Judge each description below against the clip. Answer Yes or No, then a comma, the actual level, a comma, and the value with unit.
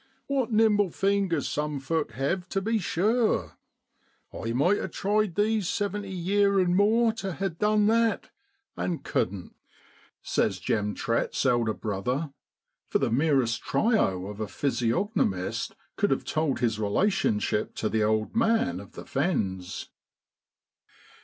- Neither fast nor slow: Yes, average, 145 wpm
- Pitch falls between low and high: Yes, medium, 175 Hz